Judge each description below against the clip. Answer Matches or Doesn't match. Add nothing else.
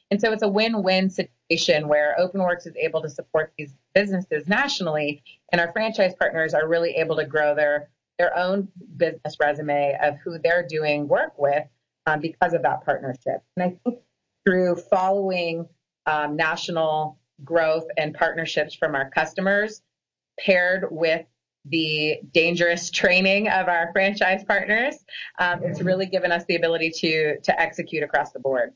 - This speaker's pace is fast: Doesn't match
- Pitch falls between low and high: Matches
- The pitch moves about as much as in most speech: Matches